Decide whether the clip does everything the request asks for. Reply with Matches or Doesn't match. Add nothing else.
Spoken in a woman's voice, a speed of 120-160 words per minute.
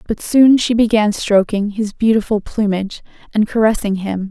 Matches